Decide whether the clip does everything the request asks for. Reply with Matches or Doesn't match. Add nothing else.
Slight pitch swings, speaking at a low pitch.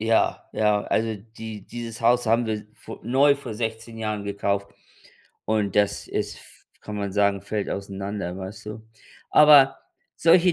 Matches